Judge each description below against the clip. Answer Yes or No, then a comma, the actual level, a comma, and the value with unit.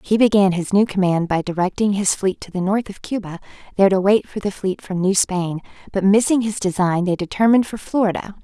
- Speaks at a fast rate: Yes, fast, 220 wpm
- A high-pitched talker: Yes, high, 195 Hz